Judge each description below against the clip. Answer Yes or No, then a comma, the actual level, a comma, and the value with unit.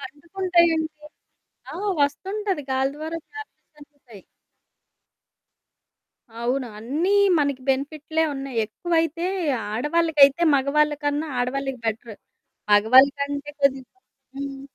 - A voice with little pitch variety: No, average, 3.3 semitones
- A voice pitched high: Yes, very high, 285 Hz